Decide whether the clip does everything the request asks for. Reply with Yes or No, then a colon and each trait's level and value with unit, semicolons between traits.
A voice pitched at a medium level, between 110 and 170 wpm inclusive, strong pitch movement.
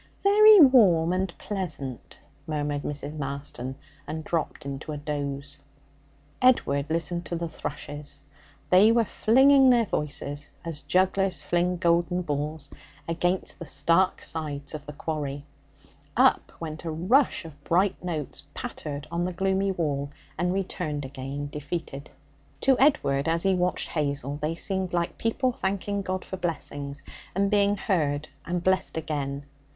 No: medium, 165 Hz; average, 140 wpm; average, 4.6 semitones